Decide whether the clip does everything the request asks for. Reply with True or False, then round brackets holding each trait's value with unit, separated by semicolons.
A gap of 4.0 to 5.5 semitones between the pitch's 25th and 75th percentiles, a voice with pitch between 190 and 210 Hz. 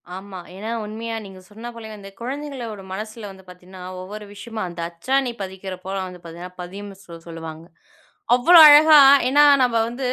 True (4.3 semitones; 205 Hz)